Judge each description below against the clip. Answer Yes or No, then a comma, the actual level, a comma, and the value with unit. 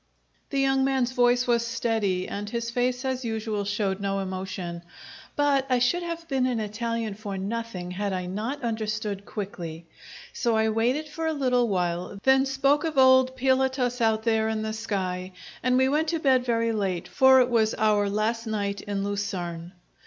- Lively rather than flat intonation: No, average, 4.3 semitones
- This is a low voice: No, high, 225 Hz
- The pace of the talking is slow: No, average, 180 wpm